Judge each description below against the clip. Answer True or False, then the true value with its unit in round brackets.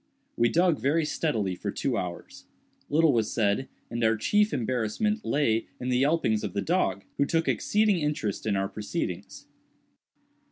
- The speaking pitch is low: True (130 Hz)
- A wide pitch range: True (7.0 semitones)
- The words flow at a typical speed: True (160 wpm)